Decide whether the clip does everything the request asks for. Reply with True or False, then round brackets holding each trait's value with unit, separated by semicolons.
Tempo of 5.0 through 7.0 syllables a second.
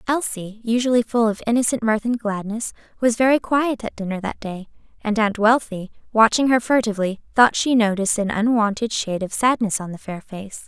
True (5.5 syllables/s)